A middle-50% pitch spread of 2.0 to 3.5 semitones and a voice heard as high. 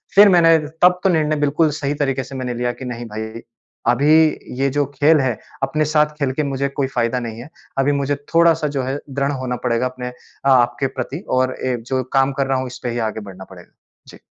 No: average, 2.8 semitones; low, 135 Hz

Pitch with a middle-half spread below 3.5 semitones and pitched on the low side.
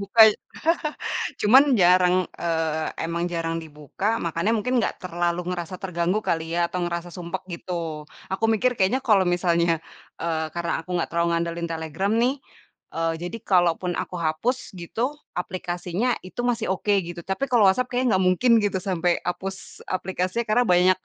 No: average, 2.8 semitones; medium, 180 Hz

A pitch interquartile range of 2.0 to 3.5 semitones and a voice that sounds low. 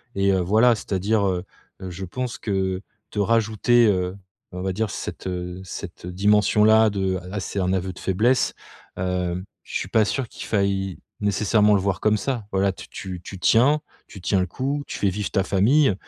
Yes: average, 2.8 semitones; low, 100 Hz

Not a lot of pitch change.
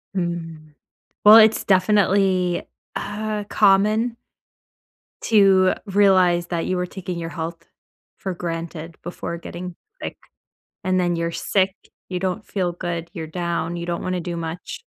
Yes: narrow, 2.3 semitones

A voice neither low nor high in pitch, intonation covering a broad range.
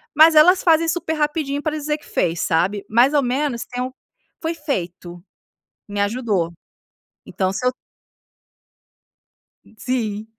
No: very high, 255 Hz; wide, 6.9 semitones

